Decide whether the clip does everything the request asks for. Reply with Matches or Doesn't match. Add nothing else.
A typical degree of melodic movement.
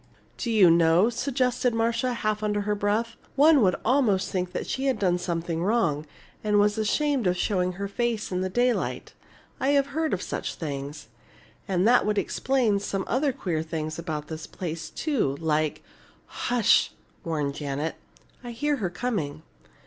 Doesn't match